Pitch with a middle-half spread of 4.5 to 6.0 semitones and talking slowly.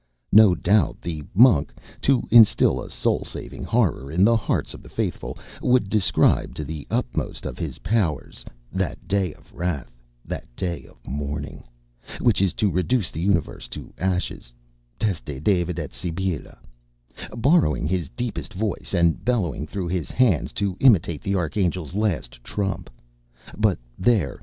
No: average, 5.1 semitones; average, 150 wpm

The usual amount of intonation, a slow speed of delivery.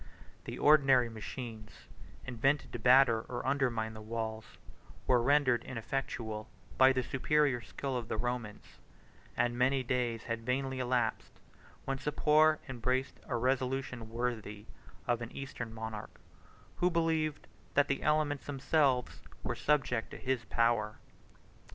Yes: average, 3.0 semitones; slow, 130 wpm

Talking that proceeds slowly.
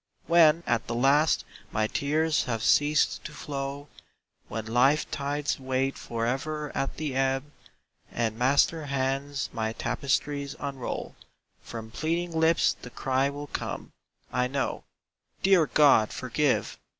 Yes: slow, 125 wpm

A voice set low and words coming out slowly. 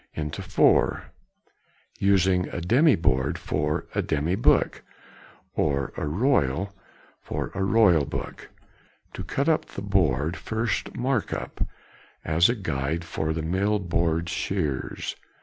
Yes: very low, 85 Hz; slow, 130 wpm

